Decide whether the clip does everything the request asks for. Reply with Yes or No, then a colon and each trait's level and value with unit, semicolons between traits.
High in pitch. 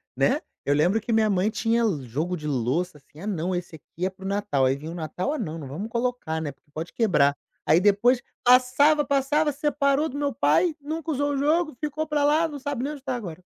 Yes: high, 225 Hz